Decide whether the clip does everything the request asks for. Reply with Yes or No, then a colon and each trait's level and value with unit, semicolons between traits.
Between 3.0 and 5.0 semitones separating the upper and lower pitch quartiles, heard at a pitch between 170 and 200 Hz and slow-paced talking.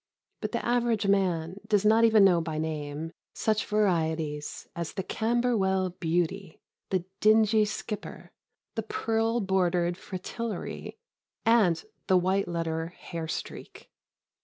Yes: average, 4.4 semitones; high, 190 Hz; slow, 115 wpm